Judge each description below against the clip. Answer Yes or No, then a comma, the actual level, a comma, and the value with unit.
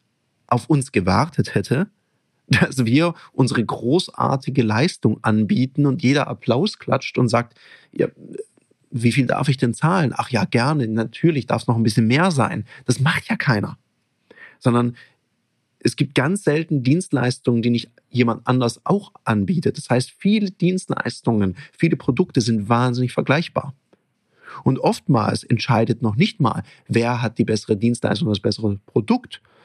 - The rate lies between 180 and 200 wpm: No, average, 150 wpm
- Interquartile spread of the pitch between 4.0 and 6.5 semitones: Yes, average, 4.3 semitones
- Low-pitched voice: Yes, low, 125 Hz